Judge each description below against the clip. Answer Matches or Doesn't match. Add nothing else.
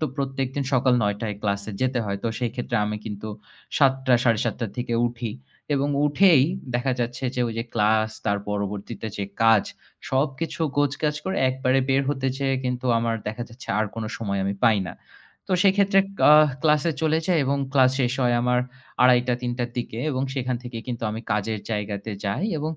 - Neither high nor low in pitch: Doesn't match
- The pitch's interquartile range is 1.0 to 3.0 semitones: Doesn't match